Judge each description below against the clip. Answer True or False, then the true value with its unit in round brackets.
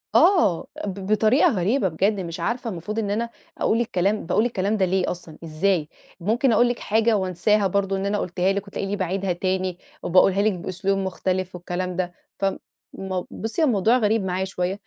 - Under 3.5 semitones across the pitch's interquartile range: True (2.7 semitones)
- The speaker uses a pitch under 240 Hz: True (195 Hz)